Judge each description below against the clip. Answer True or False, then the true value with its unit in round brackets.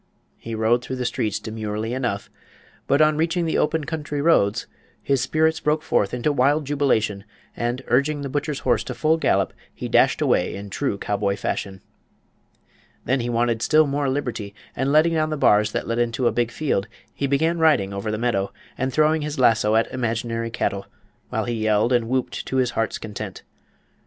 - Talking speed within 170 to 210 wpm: True (185 wpm)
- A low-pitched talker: True (125 Hz)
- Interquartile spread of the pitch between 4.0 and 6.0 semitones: True (4.9 semitones)